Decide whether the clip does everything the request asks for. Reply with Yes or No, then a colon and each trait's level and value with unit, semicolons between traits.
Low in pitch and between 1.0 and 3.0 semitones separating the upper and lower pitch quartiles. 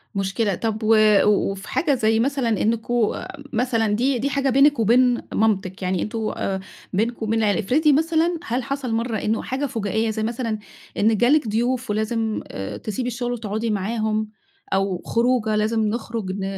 No: high, 225 Hz; narrow, 2.6 semitones